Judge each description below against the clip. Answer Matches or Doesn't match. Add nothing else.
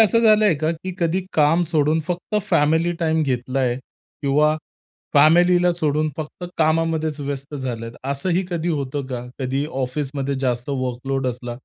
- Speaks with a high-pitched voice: Doesn't match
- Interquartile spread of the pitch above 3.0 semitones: Matches